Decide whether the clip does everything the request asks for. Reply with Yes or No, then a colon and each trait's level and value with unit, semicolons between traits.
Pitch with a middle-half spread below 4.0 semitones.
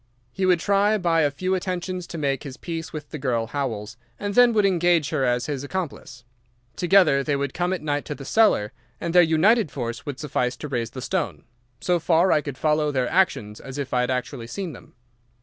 No: wide, 5.4 semitones